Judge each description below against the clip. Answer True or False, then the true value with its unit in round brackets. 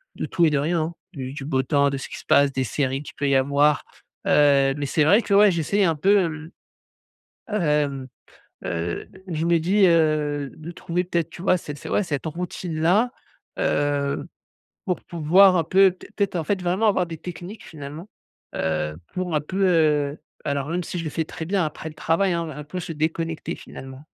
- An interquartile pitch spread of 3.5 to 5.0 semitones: True (3.8 semitones)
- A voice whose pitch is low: False (160 Hz)